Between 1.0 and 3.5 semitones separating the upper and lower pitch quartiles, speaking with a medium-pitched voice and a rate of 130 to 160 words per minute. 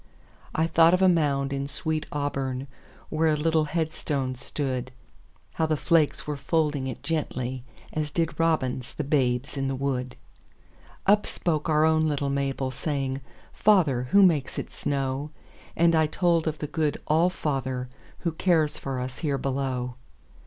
Yes: average, 3.1 semitones; medium, 145 Hz; average, 140 wpm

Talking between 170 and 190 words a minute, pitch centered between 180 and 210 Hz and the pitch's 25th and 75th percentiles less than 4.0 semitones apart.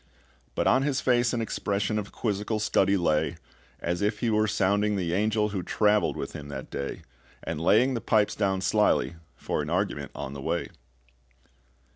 No: average, 175 wpm; low, 105 Hz; average, 3.6 semitones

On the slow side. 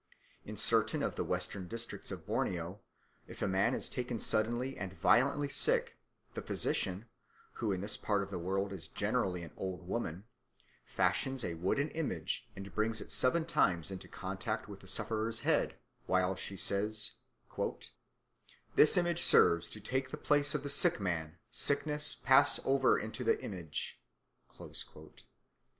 No: average, 155 wpm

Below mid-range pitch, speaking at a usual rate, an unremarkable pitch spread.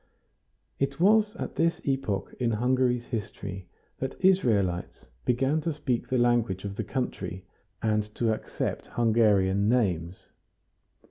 No: low, 120 Hz; slow, 125 wpm; average, 4.9 semitones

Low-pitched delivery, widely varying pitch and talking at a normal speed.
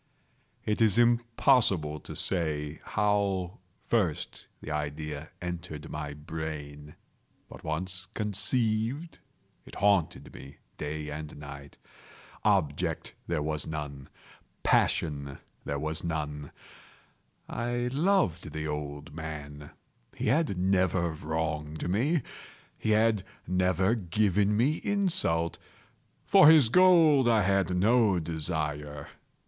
No: very low, 85 Hz; wide, 6.2 semitones; slow, 105 wpm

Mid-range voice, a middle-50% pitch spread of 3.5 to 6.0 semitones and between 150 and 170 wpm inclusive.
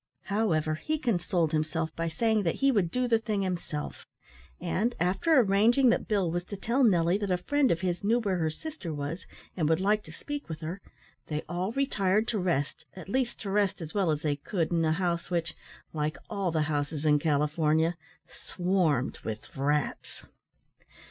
No: medium, 180 Hz; average, 5.0 semitones; average, 190 wpm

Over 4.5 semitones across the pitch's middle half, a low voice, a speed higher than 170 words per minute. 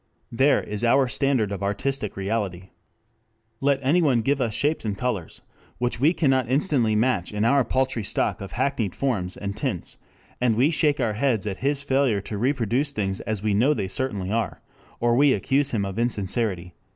Yes: average, 5.0 semitones; low, 120 Hz; average, 180 wpm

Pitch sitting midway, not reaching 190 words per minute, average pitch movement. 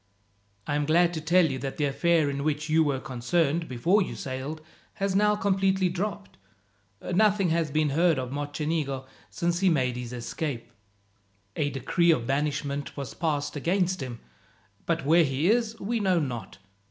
Yes: medium, 155 Hz; average, 165 wpm; average, 4.3 semitones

